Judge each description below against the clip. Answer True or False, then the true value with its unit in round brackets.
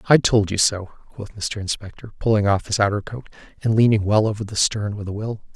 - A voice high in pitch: False (105 Hz)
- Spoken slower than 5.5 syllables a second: False (5.6 syllables/s)